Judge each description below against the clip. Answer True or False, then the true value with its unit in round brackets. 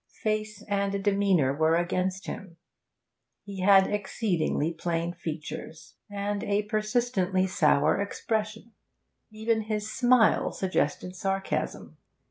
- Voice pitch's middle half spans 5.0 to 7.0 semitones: False (3.3 semitones)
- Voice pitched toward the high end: True (195 Hz)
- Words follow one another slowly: True (100 wpm)